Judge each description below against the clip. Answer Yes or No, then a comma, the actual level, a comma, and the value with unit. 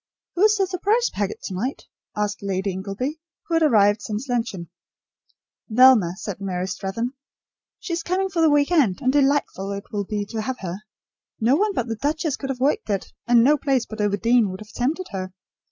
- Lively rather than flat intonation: Yes, wide, 6.5 semitones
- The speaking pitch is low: No, high, 235 Hz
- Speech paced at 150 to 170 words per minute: No, average, 200 wpm